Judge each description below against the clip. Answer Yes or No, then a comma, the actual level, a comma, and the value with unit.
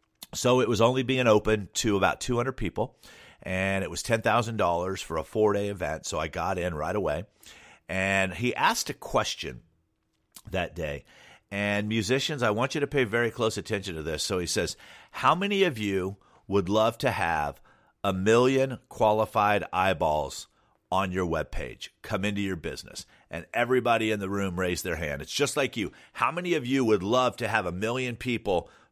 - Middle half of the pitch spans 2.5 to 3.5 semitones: No, average, 4.1 semitones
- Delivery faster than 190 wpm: No, average, 185 wpm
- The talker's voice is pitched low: Yes, low, 110 Hz